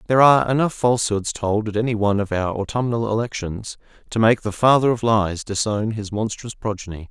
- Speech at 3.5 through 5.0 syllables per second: No, 5.8 syllables/s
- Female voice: No, male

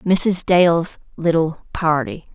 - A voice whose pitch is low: No, medium, 165 Hz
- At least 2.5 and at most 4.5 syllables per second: Yes, 3.7 syllables/s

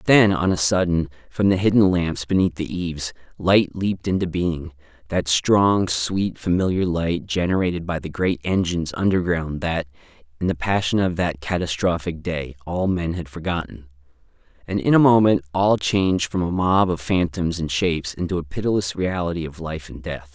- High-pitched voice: No, very low, 85 Hz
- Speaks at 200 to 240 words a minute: No, average, 170 wpm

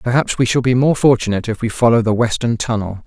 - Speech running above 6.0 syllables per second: Yes, 6.4 syllables/s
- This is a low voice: Yes, low, 120 Hz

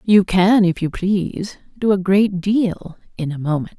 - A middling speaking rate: Yes, average, 190 wpm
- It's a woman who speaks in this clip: Yes, female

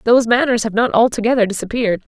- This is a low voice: No, high, 230 Hz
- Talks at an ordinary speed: Yes, average, 170 wpm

